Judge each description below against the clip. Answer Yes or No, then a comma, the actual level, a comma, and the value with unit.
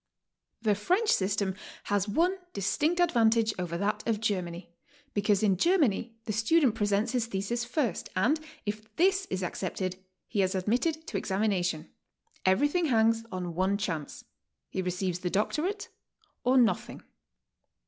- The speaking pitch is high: Yes, high, 210 Hz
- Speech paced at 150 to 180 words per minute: No, average, 140 wpm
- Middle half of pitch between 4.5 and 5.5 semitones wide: Yes, average, 5.0 semitones